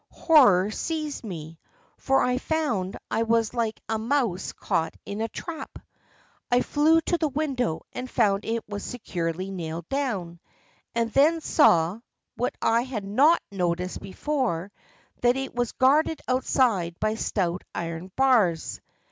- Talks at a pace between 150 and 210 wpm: No, average, 140 wpm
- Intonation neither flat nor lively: No, wide, 6.5 semitones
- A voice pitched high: Yes, high, 225 Hz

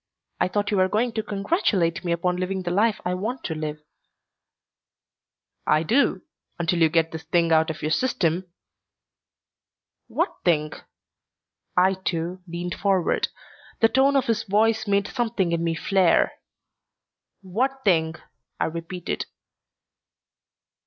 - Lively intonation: No, average, 4.1 semitones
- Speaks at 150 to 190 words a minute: No, average, 140 wpm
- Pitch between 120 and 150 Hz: No, medium, 185 Hz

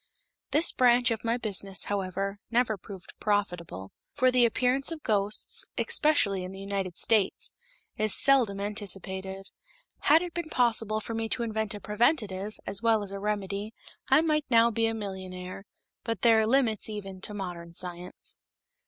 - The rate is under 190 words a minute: Yes, average, 160 wpm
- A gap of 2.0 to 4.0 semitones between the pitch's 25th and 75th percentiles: Yes, average, 3.3 semitones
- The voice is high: Yes, high, 210 Hz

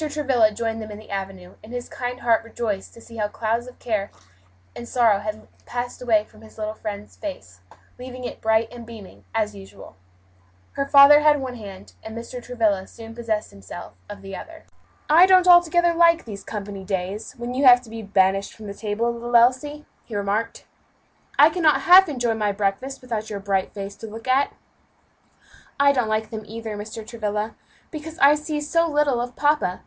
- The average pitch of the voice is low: No, high, 230 Hz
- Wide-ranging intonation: No, average, 3.9 semitones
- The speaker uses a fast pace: No, average, 195 wpm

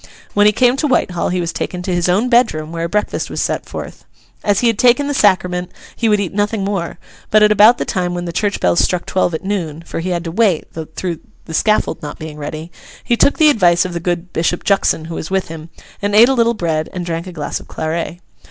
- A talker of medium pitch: Yes, medium, 180 Hz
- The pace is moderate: No, fast, 250 wpm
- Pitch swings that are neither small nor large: Yes, average, 3.8 semitones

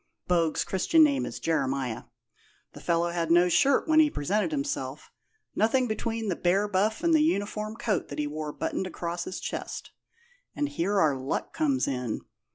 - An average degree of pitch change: No, wide, 8.1 semitones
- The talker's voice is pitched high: Yes, high, 195 Hz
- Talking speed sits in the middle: Yes, average, 170 wpm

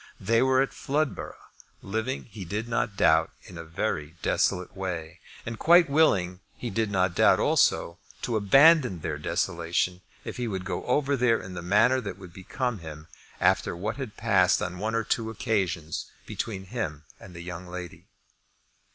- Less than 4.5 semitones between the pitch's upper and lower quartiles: No, average, 4.9 semitones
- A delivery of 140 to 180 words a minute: Yes, average, 170 wpm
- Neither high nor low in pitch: No, very low, 95 Hz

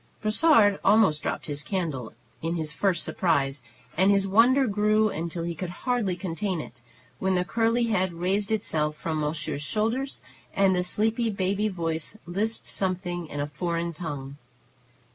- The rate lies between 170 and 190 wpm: No, average, 155 wpm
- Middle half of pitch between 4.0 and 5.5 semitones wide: Yes, average, 4.5 semitones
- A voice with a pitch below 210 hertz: Yes, medium, 185 Hz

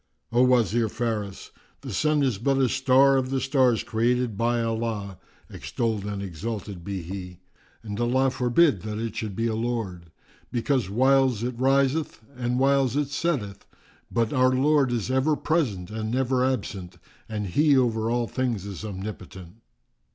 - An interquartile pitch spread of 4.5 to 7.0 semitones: No, average, 4.0 semitones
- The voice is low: Yes, low, 120 Hz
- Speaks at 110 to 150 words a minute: No, average, 160 wpm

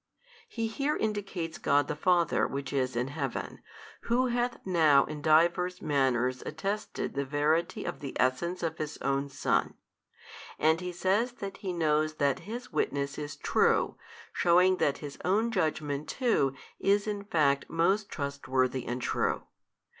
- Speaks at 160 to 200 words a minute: No, average, 150 wpm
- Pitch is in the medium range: Yes, medium, 155 Hz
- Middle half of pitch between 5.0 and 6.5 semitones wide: Yes, wide, 5.5 semitones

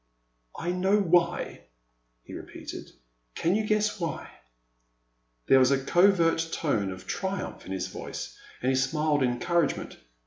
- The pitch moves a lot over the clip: Yes, wide, 6.7 semitones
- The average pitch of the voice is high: No, medium, 160 Hz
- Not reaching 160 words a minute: Yes, average, 140 wpm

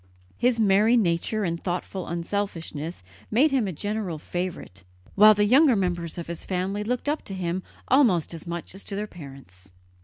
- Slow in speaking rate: No, average, 175 wpm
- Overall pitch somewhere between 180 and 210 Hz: Yes, high, 190 Hz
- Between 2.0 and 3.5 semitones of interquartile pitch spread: No, average, 4.1 semitones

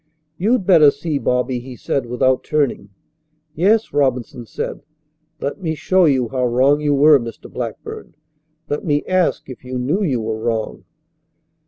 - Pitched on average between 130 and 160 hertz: Yes, medium, 140 Hz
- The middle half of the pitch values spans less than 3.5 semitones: No, average, 4.0 semitones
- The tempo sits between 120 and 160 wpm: Yes, average, 155 wpm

